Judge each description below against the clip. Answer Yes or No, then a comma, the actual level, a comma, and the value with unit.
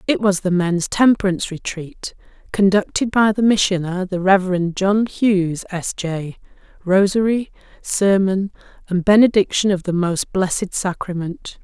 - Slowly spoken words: Yes, slow, 130 wpm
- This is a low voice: No, high, 190 Hz